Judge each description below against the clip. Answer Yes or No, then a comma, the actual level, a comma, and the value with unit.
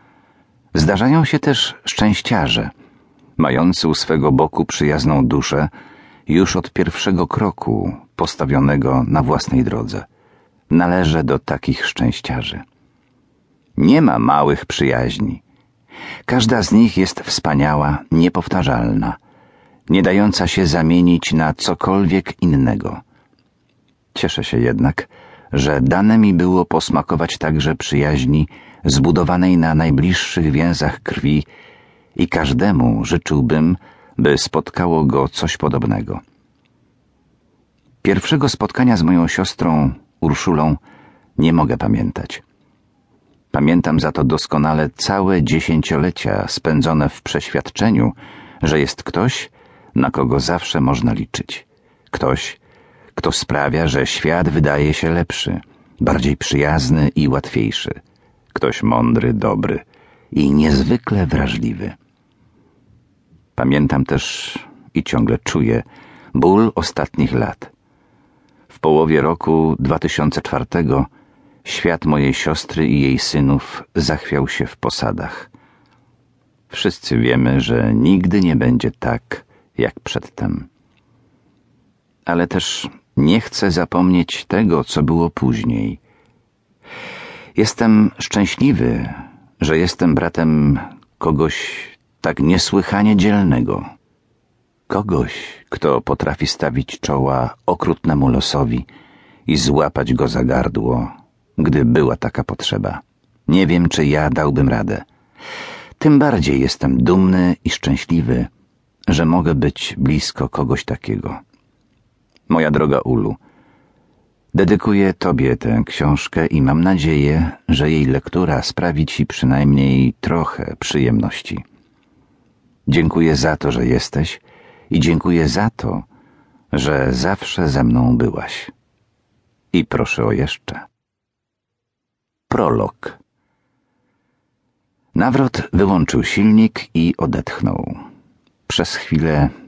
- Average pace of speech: No, slow, 100 wpm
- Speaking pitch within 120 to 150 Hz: No, very low, 80 Hz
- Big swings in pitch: No, average, 4.0 semitones